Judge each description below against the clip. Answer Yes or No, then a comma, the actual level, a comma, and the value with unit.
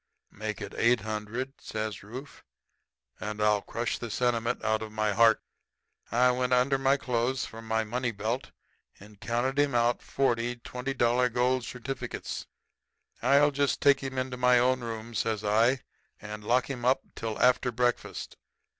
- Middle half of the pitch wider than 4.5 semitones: No, narrow, 2.6 semitones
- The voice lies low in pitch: Yes, low, 120 Hz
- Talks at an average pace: Yes, average, 160 wpm